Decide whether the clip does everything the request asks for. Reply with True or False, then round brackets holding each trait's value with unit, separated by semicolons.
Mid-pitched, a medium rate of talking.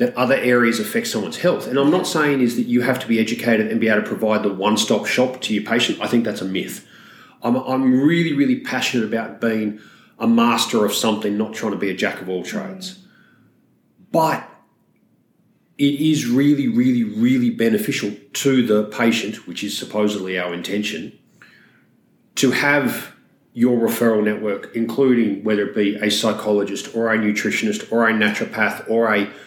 False (115 Hz; 170 wpm)